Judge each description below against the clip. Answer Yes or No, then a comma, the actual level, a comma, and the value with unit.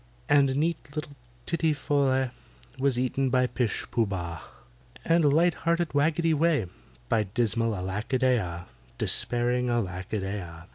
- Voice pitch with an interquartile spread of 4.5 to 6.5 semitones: Yes, wide, 5.6 semitones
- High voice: No, low, 125 Hz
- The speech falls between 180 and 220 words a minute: No, average, 155 wpm